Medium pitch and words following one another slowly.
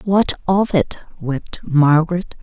Yes: medium, 170 Hz; slow, 125 wpm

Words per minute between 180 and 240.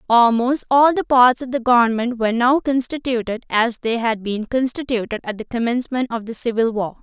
Yes: average, 190 wpm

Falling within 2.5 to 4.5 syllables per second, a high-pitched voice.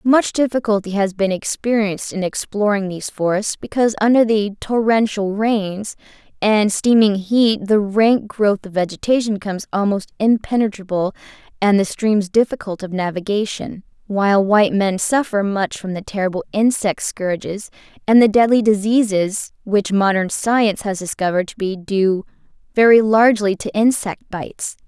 No: 5.0 syllables/s; high, 205 Hz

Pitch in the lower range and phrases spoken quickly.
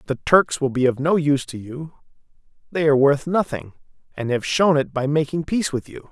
No: medium, 145 Hz; fast, 215 wpm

